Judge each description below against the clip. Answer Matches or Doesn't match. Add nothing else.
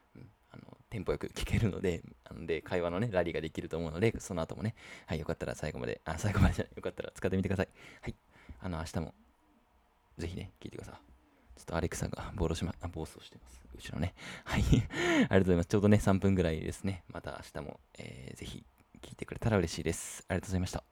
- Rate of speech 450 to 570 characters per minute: Matches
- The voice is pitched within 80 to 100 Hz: Matches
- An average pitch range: Matches